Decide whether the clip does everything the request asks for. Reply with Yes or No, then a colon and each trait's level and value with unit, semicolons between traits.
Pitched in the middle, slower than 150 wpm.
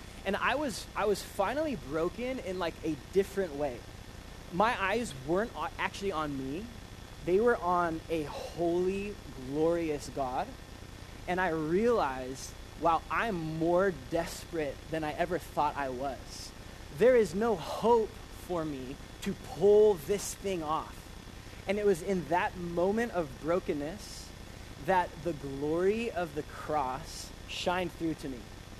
Yes: medium, 165 Hz; average, 140 wpm